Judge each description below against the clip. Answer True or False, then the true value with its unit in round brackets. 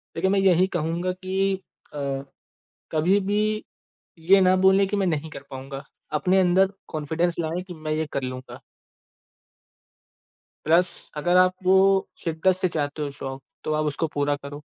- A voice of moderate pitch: True (170 Hz)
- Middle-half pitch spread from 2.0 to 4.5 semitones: True (3.8 semitones)